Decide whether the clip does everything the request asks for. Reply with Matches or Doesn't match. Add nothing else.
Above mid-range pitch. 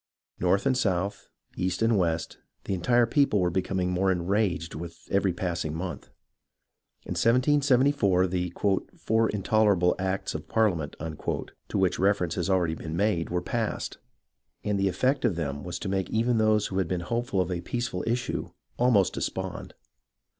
Doesn't match